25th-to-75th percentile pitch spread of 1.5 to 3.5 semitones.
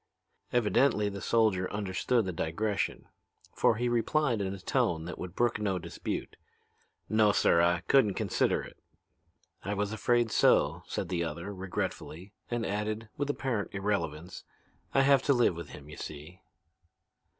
No: average, 4.2 semitones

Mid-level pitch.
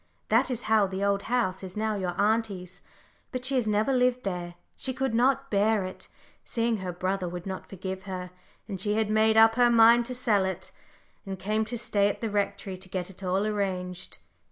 No: high, 205 Hz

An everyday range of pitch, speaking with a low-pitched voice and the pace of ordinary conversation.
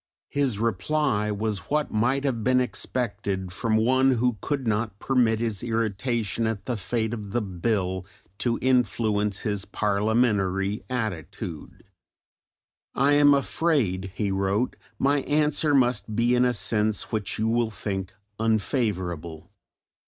No: average, 3.8 semitones; low, 110 Hz; slow, 130 wpm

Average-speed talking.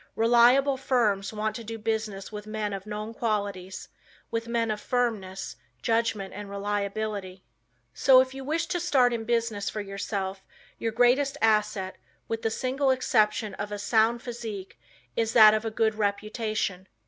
Yes: average, 160 wpm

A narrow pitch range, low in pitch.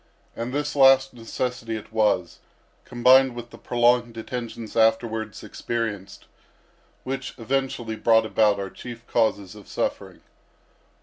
Yes: narrow, 2.1 semitones; low, 115 Hz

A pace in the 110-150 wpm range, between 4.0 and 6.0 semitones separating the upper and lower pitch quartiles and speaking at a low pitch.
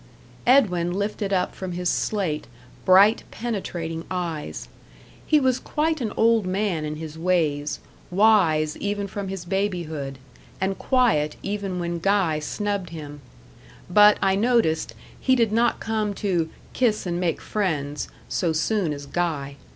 No: average, 140 wpm; average, 4.6 semitones; medium, 185 Hz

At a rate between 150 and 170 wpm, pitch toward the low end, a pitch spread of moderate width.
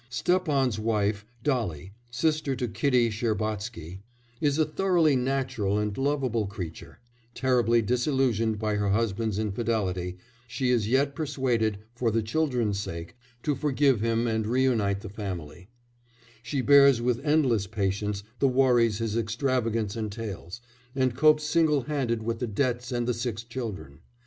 No: average, 140 wpm; low, 115 Hz; average, 3.9 semitones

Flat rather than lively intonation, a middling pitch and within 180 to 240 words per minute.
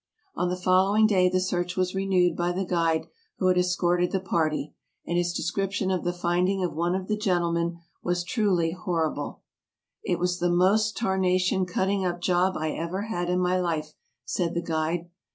Yes: narrow, 1.5 semitones; medium, 180 Hz; average, 185 wpm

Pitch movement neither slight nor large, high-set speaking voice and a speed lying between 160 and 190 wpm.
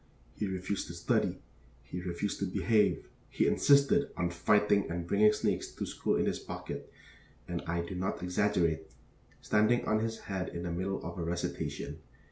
No: average, 3.3 semitones; very low, 95 Hz; average, 170 wpm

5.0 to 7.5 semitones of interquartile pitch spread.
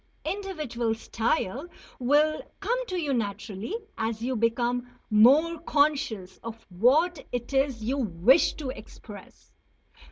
Yes: average, 5.3 semitones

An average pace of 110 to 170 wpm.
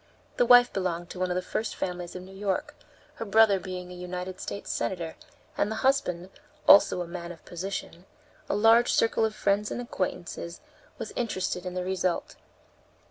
No: average, 180 wpm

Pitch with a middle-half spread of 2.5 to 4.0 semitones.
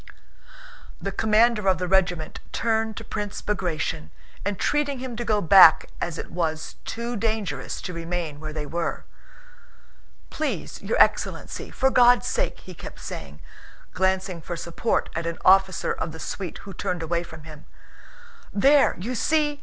No: average, 5.1 semitones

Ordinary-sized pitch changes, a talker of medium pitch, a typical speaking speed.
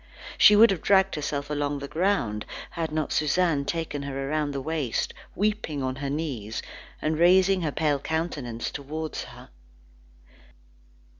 Yes: average, 3.2 semitones; medium, 150 Hz; average, 145 wpm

